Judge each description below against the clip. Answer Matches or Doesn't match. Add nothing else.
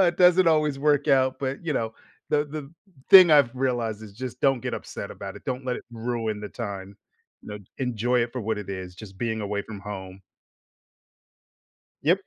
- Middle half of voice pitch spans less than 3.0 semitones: Doesn't match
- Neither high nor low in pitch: Doesn't match